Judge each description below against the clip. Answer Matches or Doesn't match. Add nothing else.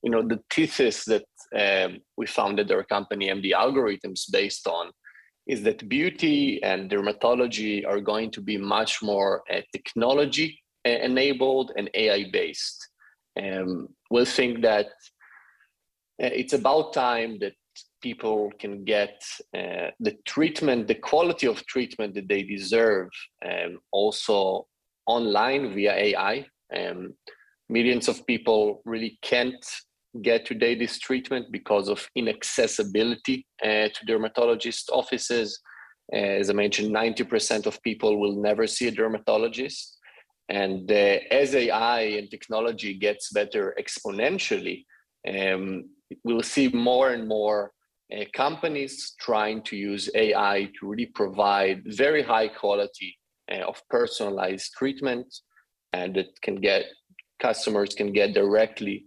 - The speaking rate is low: Matches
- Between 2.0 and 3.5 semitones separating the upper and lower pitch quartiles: Doesn't match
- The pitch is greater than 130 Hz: Doesn't match